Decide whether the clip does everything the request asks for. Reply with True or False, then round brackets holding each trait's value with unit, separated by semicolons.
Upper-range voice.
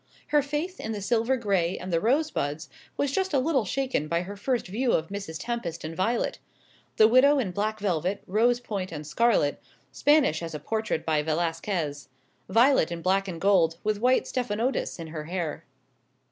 True (200 Hz)